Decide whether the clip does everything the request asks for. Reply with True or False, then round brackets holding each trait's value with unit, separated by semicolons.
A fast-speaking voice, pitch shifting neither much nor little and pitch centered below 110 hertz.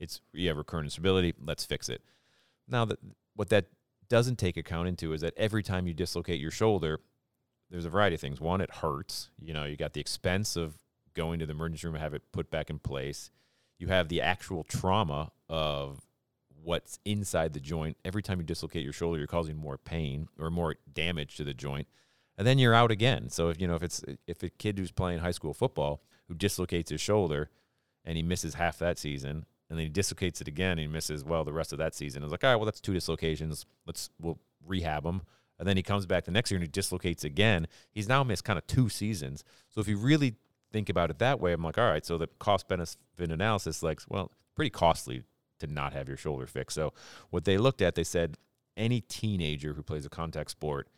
True (230 wpm; 4.4 semitones; 85 Hz)